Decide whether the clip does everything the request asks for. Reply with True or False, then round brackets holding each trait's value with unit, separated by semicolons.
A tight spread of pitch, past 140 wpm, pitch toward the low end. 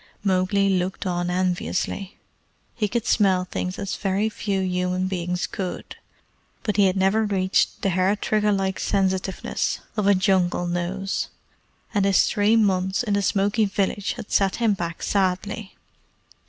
False (1.8 semitones; 150 wpm; 195 Hz)